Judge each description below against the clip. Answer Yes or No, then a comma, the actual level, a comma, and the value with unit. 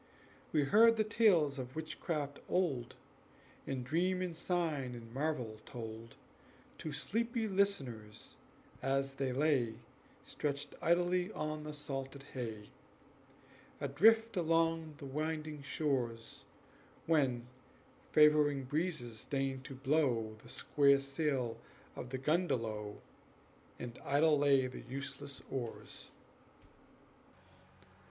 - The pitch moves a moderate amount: Yes, average, 3.9 semitones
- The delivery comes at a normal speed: No, slow, 105 wpm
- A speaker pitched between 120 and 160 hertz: Yes, medium, 140 Hz